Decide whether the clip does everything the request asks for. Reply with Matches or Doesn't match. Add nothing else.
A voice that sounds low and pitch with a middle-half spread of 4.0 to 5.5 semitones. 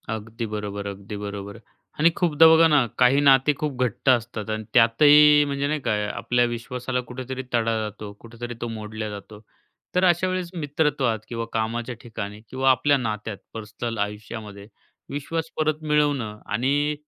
Matches